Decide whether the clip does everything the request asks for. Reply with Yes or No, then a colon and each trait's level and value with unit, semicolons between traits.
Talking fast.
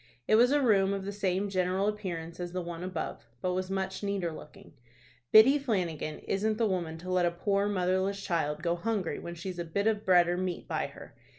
Yes: fast, 215 wpm